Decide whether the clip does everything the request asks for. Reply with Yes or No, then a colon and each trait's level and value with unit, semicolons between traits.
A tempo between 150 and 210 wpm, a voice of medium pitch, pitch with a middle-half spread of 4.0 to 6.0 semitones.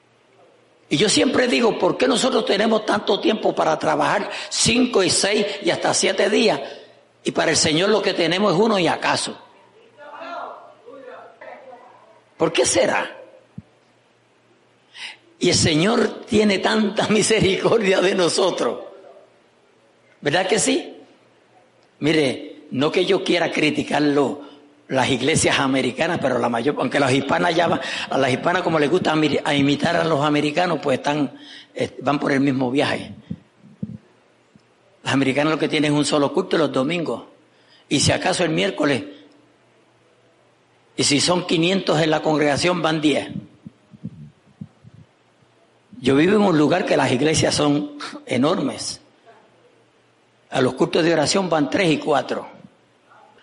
No: average, 140 wpm; medium, 160 Hz; average, 5.2 semitones